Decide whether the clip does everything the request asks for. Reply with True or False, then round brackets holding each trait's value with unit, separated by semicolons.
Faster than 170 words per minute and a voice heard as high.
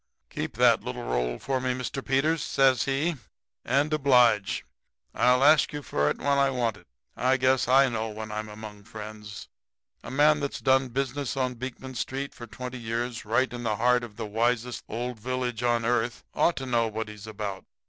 False (190 wpm; 125 Hz)